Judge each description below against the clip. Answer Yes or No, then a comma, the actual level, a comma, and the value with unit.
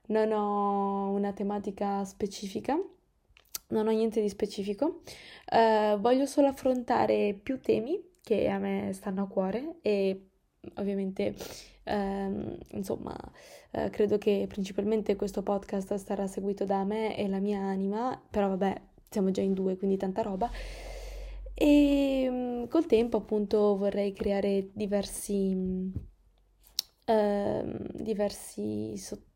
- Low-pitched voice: No, high, 205 Hz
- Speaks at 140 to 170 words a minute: No, average, 125 wpm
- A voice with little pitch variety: Yes, narrow, 2.2 semitones